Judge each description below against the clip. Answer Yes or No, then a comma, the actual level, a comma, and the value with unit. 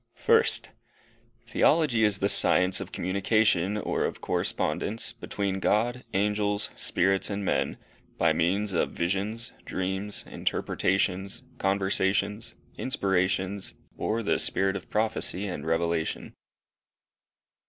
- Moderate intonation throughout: No, narrow, 2.1 semitones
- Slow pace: Yes, slow, 105 wpm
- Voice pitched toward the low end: Yes, low, 100 Hz